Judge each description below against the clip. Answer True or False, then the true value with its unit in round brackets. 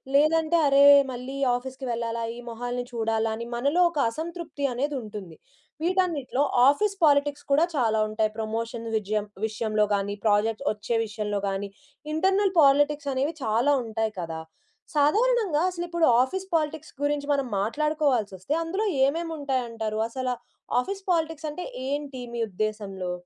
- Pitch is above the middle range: True (265 Hz)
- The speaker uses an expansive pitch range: True (5.8 semitones)